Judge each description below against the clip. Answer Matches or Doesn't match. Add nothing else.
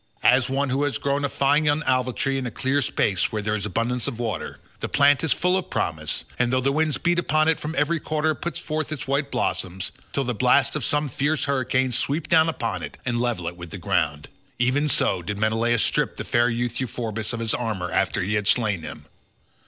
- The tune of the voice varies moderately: Matches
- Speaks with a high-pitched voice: Doesn't match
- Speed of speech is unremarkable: Doesn't match